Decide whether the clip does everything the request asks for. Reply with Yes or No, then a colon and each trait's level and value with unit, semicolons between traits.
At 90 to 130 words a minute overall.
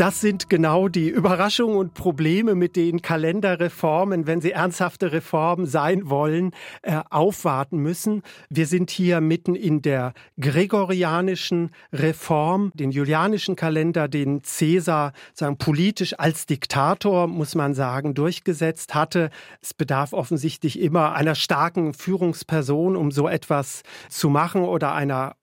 Yes: slow, 125 wpm